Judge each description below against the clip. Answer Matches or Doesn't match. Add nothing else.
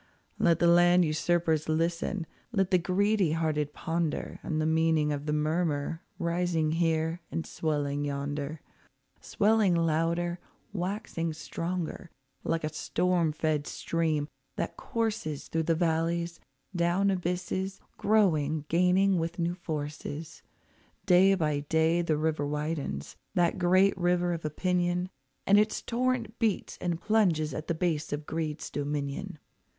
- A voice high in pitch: Doesn't match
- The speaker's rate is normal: Doesn't match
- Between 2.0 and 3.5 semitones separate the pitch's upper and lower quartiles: Matches